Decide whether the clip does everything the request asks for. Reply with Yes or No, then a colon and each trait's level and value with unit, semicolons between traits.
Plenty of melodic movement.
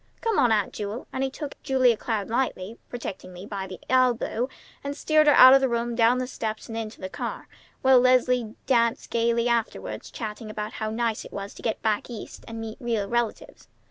No: average, 2.7 semitones